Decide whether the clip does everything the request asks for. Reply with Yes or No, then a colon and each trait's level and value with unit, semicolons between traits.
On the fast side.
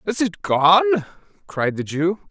No: average, 155 wpm